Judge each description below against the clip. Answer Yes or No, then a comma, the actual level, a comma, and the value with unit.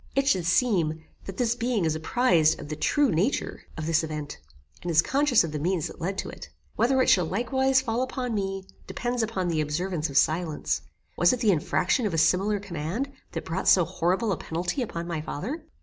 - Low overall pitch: No, medium, 185 Hz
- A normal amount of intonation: No, wide, 6.7 semitones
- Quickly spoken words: Yes, fast, 210 wpm